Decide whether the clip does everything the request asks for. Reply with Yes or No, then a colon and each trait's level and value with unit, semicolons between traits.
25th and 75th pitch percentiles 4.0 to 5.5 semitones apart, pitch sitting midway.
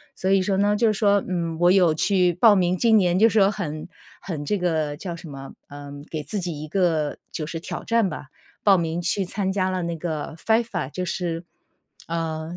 No: average, 3.5 semitones; medium, 175 Hz